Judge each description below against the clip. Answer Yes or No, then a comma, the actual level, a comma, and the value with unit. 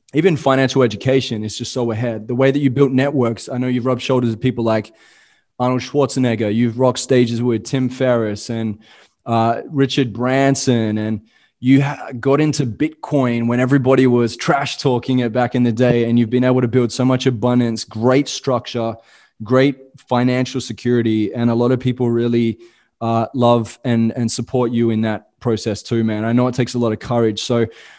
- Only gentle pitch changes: Yes, narrow, 2.0 semitones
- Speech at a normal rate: Yes, average, 180 wpm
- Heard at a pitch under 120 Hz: No, low, 125 Hz